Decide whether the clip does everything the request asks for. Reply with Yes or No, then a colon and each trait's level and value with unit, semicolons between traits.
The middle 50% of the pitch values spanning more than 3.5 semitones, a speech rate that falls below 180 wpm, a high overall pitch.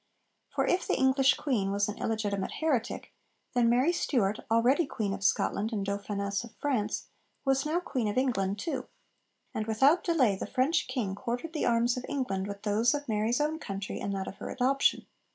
No: average, 5.0 semitones; average, 190 wpm; high, 235 Hz